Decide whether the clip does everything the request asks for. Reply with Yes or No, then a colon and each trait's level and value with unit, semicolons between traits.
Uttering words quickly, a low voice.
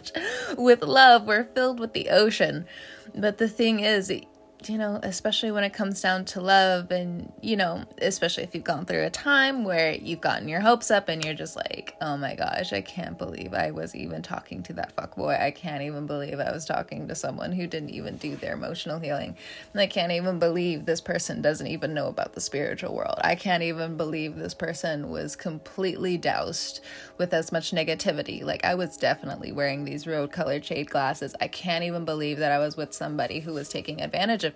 No: fast, 210 wpm; medium, 175 Hz